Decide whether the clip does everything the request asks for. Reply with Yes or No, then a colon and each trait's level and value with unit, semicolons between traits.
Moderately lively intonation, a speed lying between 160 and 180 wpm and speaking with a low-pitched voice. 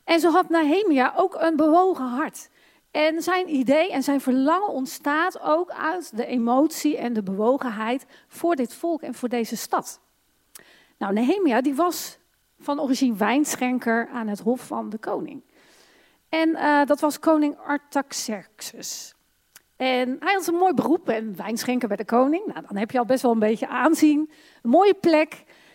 No: average, 4.7 semitones; average, 170 wpm; very high, 290 Hz